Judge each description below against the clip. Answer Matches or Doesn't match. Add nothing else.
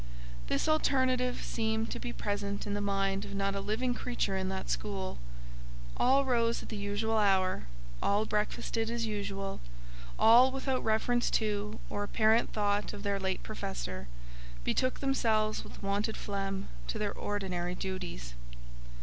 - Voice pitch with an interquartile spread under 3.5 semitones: Matches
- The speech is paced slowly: Doesn't match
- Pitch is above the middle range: Matches